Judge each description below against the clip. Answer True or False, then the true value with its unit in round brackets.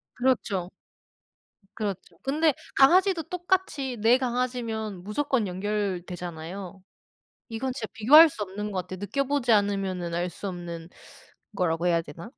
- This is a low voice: False (210 Hz)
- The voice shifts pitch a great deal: True (6.3 semitones)